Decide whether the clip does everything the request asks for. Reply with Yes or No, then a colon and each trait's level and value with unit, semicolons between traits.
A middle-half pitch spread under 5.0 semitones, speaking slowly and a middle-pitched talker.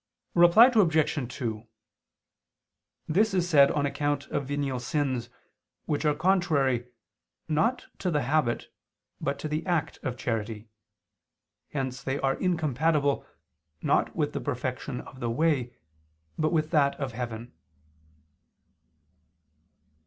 Yes: average, 4.0 semitones; slow, 120 wpm; medium, 145 Hz